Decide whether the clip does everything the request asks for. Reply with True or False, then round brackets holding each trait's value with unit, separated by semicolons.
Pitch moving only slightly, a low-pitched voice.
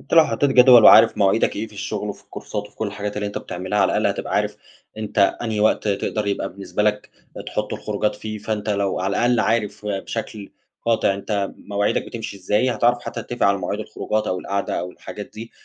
True (1.7 semitones; 105 Hz)